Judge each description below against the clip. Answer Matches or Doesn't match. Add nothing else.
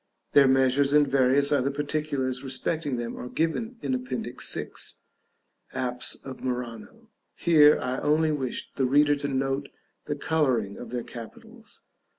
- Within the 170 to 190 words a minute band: Doesn't match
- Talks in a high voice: Doesn't match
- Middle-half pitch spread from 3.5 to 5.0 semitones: Doesn't match